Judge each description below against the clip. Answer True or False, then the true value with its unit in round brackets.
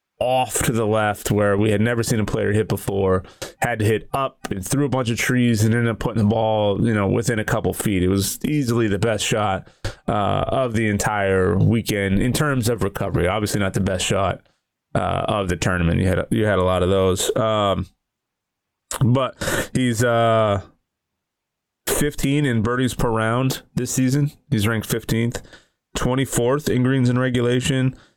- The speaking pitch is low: True (110 Hz)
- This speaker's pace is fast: False (185 wpm)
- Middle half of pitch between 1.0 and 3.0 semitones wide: False (3.8 semitones)